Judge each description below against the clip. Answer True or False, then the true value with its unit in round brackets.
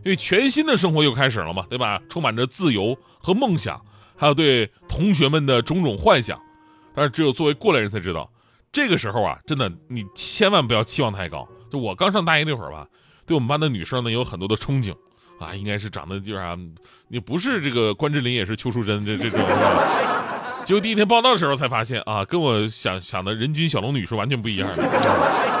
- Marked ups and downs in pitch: True (6.6 semitones)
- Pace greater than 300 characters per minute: True (335 characters per minute)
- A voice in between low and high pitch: False (125 Hz)